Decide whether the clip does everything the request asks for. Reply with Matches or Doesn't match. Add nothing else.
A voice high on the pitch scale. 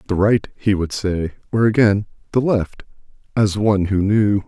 Doesn't match